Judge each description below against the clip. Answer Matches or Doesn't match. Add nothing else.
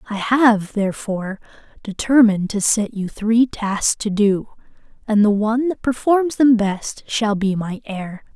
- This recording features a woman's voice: Matches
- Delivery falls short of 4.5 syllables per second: Matches